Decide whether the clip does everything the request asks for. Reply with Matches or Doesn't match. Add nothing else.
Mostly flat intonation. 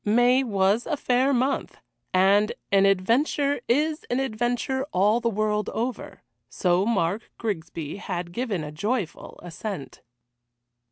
Doesn't match